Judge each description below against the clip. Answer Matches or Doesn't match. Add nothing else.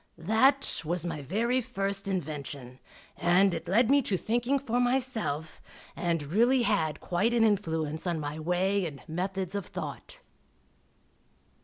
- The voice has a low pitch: Doesn't match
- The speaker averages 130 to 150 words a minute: Matches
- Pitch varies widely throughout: Matches